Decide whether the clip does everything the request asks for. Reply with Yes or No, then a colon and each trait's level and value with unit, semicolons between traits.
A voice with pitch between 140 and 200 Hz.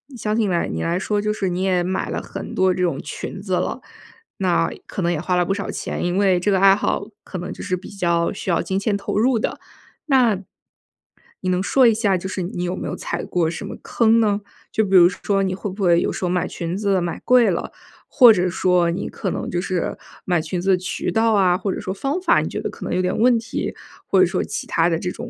Yes: high, 190 Hz